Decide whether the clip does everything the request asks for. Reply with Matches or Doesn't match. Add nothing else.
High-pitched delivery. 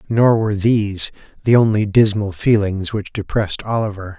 Doesn't match